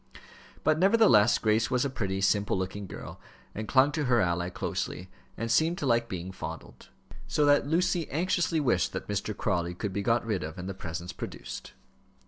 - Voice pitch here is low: Yes, low, 110 Hz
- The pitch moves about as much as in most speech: No, wide, 7.1 semitones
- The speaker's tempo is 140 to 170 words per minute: No, average, 185 wpm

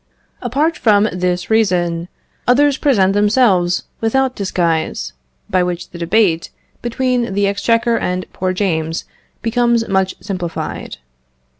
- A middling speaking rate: No, slow, 115 wpm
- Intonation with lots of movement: No, average, 4.7 semitones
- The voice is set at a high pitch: Yes, high, 200 Hz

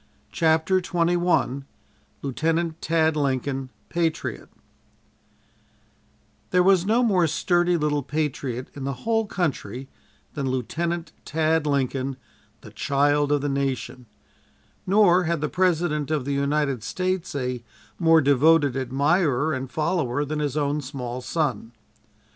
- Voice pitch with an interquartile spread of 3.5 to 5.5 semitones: Yes, average, 3.8 semitones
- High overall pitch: No, medium, 150 Hz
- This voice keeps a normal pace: No, slow, 120 wpm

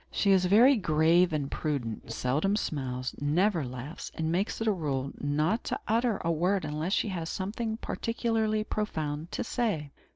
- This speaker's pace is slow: No, average, 165 wpm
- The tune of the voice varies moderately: No, wide, 6.2 semitones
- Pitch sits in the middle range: Yes, medium, 170 Hz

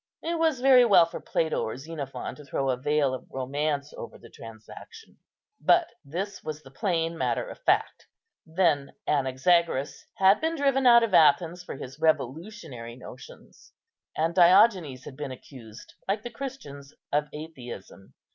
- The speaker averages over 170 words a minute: No, average, 155 wpm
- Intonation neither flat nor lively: No, wide, 6.6 semitones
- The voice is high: No, medium, 160 Hz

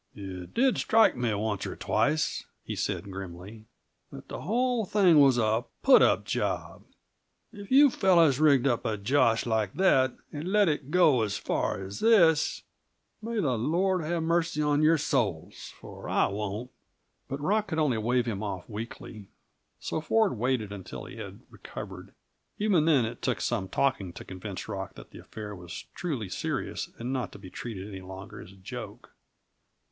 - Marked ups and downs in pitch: Yes, wide, 8.2 semitones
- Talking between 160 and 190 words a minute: Yes, average, 175 wpm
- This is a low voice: Yes, low, 125 Hz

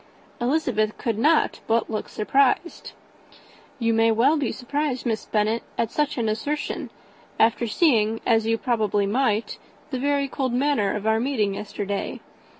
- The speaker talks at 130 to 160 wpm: Yes, average, 150 wpm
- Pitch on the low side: No, high, 230 Hz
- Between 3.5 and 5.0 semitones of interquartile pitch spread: Yes, average, 4.0 semitones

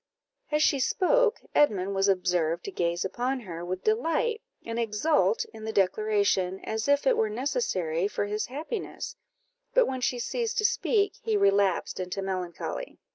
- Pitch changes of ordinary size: No, wide, 7.7 semitones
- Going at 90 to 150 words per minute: No, average, 160 wpm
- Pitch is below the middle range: No, high, 215 Hz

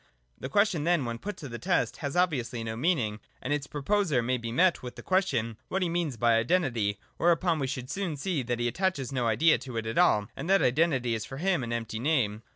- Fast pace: Yes, fast, 235 wpm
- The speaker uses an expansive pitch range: Yes, wide, 6.6 semitones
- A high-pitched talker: No, low, 135 Hz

